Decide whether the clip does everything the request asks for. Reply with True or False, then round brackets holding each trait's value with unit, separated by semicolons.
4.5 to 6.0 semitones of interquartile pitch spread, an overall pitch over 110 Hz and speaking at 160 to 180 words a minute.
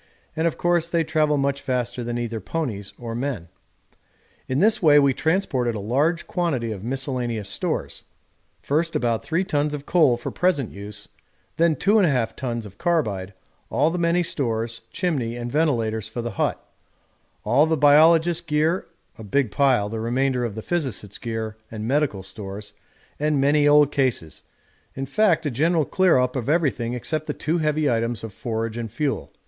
True (5.6 semitones; 135 Hz; 175 wpm)